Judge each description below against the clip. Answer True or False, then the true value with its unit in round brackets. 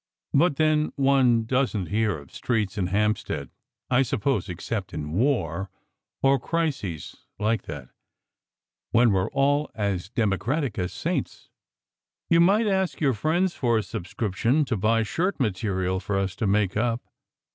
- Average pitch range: False (6.2 semitones)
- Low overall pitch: True (110 Hz)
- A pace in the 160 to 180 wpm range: False (150 wpm)